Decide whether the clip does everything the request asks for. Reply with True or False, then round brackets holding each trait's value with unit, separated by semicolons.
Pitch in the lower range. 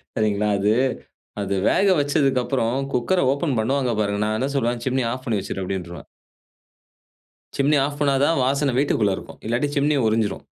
True (125 Hz)